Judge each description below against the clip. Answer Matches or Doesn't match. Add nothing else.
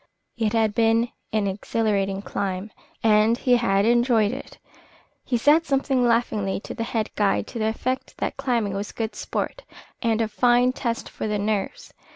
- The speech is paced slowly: Doesn't match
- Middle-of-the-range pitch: Doesn't match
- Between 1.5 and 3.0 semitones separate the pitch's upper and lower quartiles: Matches